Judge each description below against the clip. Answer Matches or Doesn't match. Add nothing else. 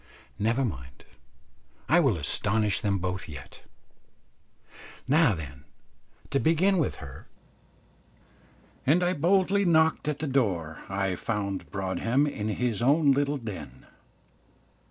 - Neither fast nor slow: Doesn't match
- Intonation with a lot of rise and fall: Matches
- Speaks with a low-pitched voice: Matches